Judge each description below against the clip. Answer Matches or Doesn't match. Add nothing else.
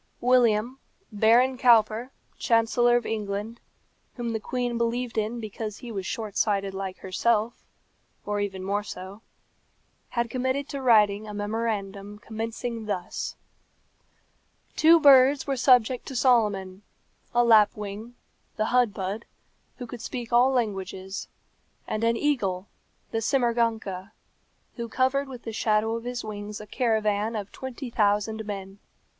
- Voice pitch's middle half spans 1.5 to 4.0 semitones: Matches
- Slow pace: Matches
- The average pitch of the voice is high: Matches